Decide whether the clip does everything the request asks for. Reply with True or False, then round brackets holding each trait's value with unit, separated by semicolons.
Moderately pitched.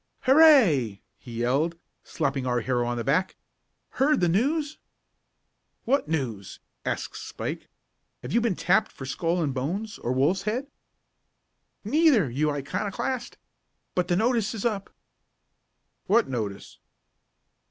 True (175 Hz)